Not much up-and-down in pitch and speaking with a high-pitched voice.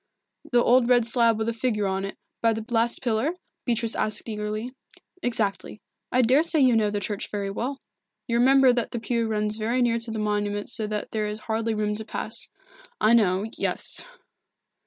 Yes: narrow, 2.2 semitones; high, 225 Hz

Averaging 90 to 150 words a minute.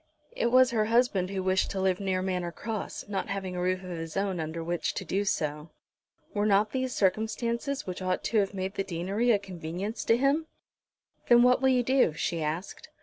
No: fast, 205 wpm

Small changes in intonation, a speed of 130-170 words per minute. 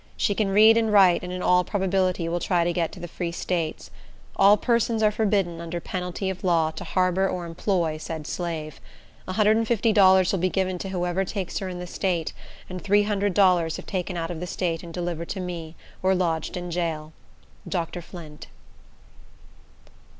No: narrow, 2.3 semitones; average, 180 wpm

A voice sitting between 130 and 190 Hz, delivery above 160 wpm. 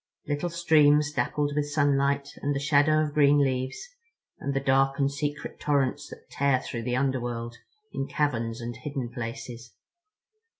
No: medium, 140 Hz; average, 155 wpm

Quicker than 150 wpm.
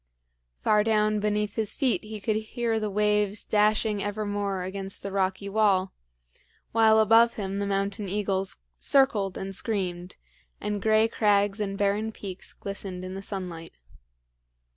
No: average, 140 wpm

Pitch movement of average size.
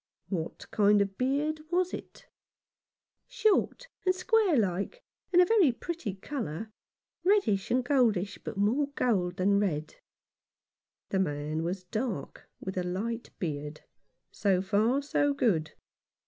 No: wide, 7.7 semitones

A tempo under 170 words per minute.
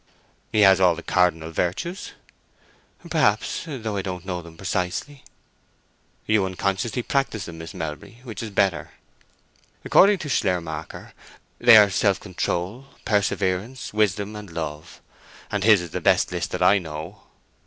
Yes: average, 140 wpm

